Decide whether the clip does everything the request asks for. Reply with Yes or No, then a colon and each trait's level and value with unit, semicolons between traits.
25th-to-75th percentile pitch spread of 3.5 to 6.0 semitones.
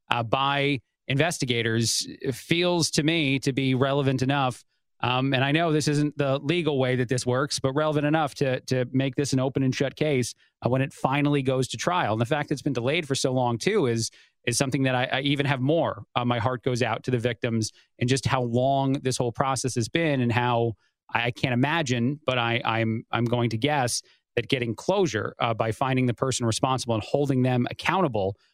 No: narrow, 2.6 semitones